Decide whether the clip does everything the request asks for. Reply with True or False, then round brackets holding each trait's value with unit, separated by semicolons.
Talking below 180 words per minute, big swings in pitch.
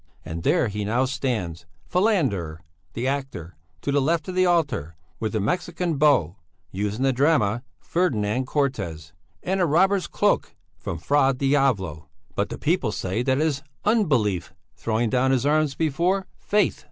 True (160 wpm; 7.4 semitones)